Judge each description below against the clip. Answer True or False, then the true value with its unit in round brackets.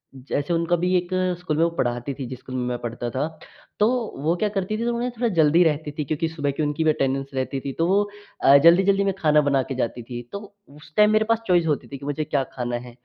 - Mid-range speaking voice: True (150 Hz)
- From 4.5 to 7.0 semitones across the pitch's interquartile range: True (5.0 semitones)